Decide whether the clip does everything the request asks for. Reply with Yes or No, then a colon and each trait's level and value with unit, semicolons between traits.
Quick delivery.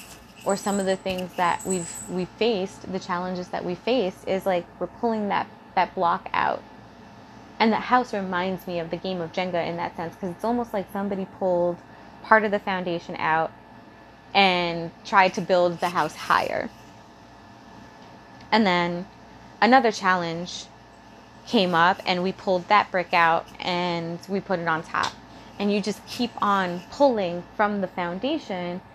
No: average, 165 wpm